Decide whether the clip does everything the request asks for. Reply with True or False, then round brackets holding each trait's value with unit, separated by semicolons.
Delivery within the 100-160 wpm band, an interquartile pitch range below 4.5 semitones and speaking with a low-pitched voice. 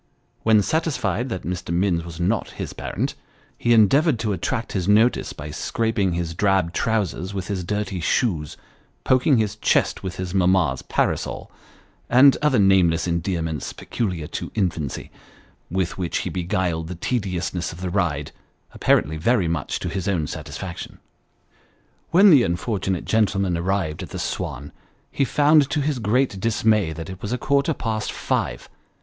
False (155 wpm; 4.8 semitones; 95 Hz)